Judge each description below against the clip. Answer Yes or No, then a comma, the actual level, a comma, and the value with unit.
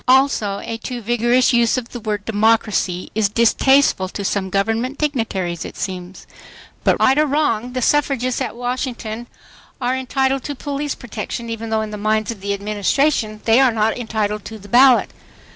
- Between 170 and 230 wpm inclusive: Yes, average, 175 wpm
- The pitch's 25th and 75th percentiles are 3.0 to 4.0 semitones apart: Yes, average, 3.4 semitones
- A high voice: Yes, high, 230 Hz